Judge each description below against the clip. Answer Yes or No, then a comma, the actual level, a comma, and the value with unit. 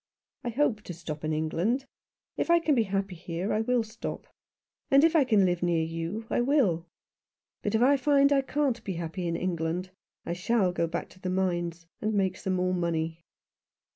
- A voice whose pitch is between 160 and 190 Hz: Yes, medium, 185 Hz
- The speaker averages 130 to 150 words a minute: No, average, 200 wpm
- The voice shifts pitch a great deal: Yes, wide, 5.9 semitones